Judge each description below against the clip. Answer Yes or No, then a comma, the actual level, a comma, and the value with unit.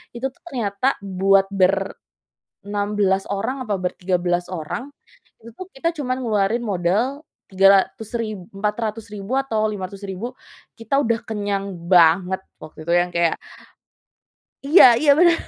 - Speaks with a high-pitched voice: Yes, high, 200 Hz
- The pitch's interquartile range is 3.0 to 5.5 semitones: Yes, average, 3.5 semitones